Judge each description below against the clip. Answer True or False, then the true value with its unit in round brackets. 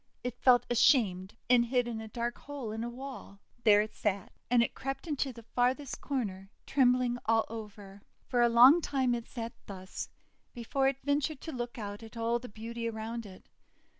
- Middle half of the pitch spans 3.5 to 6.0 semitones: False (2.5 semitones)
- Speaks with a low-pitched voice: False (235 Hz)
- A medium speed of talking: True (190 wpm)